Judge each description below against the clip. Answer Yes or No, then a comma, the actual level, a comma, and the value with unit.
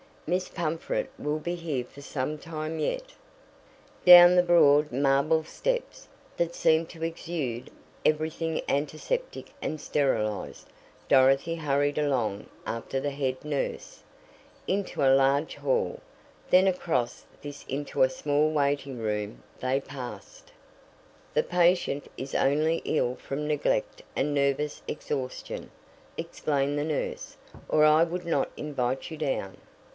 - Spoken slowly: Yes, slow, 125 wpm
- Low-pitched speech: No, medium, 150 Hz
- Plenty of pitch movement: No, average, 3.3 semitones